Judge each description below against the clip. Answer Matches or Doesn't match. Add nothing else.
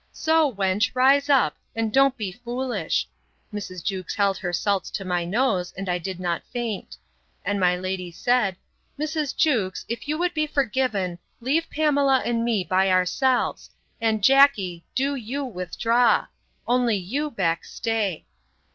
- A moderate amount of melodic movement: Doesn't match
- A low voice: Doesn't match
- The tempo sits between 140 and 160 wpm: Matches